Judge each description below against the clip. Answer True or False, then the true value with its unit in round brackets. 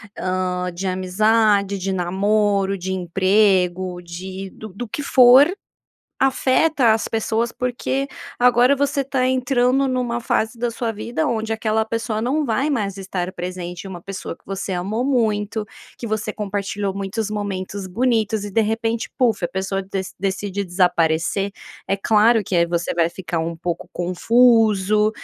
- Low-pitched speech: False (205 Hz)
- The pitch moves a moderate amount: True (3.7 semitones)